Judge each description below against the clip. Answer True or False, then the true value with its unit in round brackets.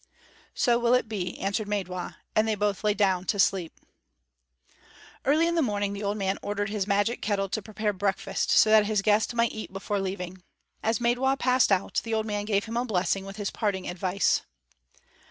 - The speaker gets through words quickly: False (195 wpm)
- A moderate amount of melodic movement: False (2.2 semitones)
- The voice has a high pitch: True (205 Hz)